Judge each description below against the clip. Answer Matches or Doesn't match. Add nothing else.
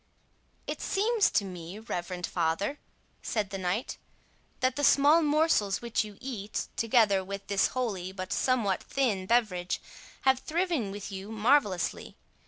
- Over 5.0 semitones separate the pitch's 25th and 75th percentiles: Matches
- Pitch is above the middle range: Matches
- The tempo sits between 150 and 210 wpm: Doesn't match